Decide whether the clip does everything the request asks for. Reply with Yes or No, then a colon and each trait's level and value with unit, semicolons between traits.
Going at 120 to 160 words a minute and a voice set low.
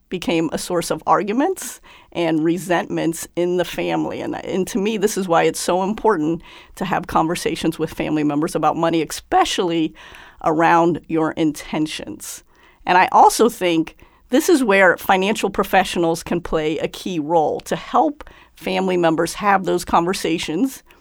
No: average, 150 wpm; medium, 175 Hz